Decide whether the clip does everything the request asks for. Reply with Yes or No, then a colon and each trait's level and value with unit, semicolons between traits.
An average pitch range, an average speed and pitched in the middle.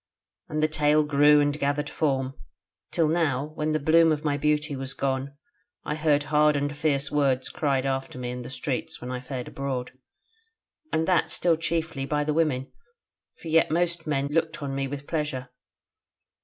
No: narrow, 2.2 semitones; average, 180 wpm; medium, 145 Hz